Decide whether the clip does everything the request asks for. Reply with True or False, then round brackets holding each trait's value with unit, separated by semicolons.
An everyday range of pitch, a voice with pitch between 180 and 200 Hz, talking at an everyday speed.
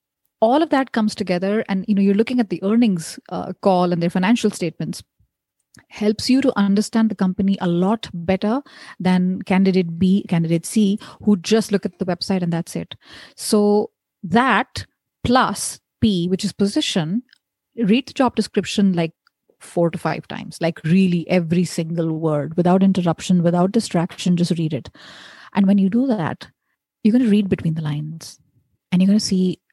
True (3.7 semitones; 190 Hz; 175 wpm)